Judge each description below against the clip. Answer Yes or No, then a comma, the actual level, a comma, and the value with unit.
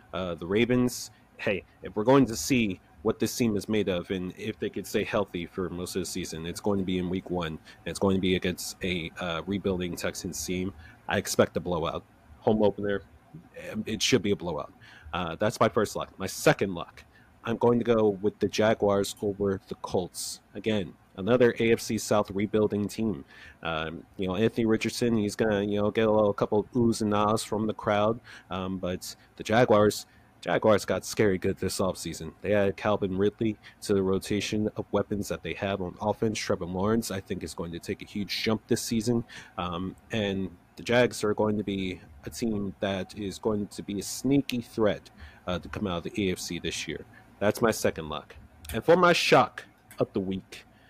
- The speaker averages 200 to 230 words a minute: Yes, fast, 205 wpm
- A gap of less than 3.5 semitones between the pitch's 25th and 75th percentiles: Yes, average, 2.9 semitones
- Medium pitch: No, low, 105 Hz